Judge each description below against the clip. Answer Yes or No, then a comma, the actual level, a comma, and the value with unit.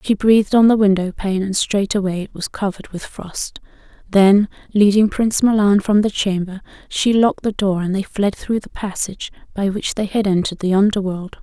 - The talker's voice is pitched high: Yes, high, 200 Hz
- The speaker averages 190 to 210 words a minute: Yes, average, 195 wpm